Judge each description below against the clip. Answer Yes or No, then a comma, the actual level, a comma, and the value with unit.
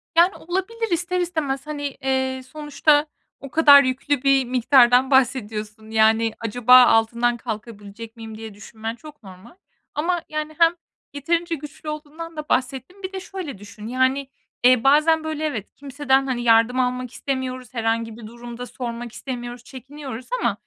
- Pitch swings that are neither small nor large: Yes, average, 4.5 semitones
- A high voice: Yes, very high, 260 Hz